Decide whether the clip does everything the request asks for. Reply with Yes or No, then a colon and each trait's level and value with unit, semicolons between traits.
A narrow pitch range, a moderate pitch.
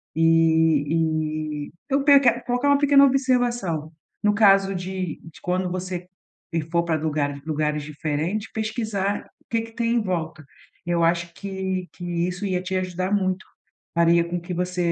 No: average, 4.2 semitones; medium, 180 Hz